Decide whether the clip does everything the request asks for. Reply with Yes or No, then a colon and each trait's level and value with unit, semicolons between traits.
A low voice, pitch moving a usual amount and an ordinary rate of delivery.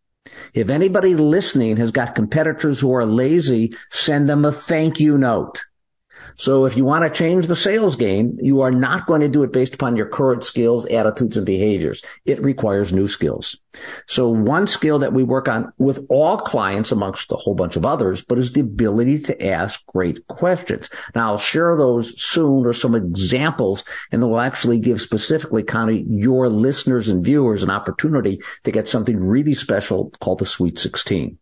Yes: low, 130 Hz; average, 4.4 semitones; average, 185 wpm